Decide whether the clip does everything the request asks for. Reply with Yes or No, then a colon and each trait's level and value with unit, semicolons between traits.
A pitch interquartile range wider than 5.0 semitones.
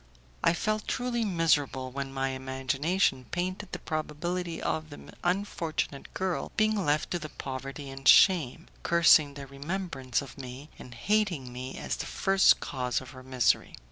Yes: wide, 5.4 semitones